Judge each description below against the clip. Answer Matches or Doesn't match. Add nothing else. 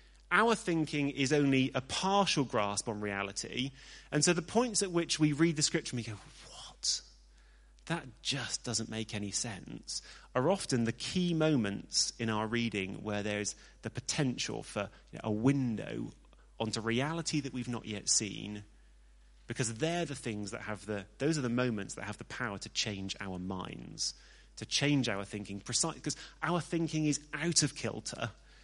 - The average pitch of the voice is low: Matches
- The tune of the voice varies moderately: Doesn't match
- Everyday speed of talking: Matches